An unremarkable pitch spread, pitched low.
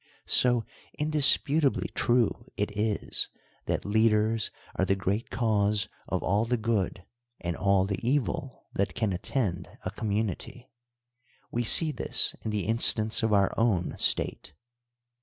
Yes: average, 3.1 semitones; low, 110 Hz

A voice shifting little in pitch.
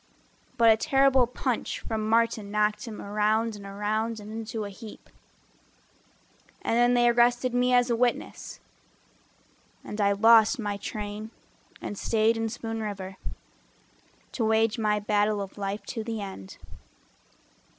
Yes: narrow, 1.9 semitones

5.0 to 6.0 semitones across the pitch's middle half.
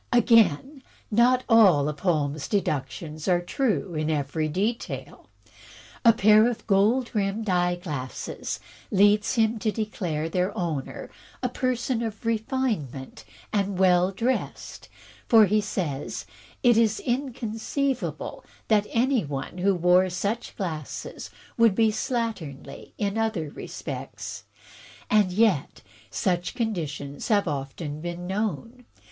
Yes: wide, 5.6 semitones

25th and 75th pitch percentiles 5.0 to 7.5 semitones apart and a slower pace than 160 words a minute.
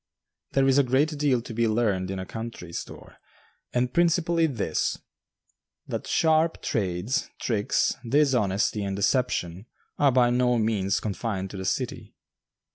Yes: wide, 5.5 semitones; average, 140 wpm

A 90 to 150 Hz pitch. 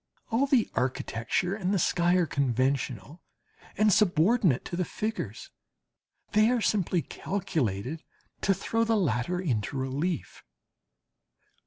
No: medium, 175 Hz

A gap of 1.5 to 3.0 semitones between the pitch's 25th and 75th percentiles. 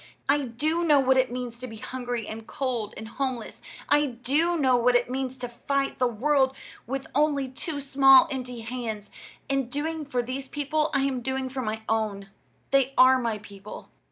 Yes: narrow, 2.5 semitones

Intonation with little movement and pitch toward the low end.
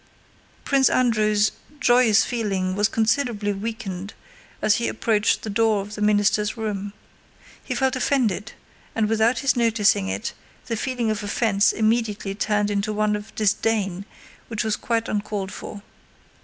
No: narrow, 1.9 semitones; high, 215 Hz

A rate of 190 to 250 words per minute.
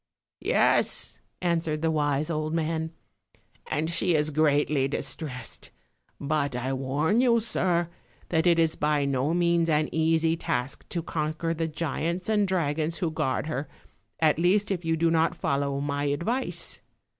No: average, 155 wpm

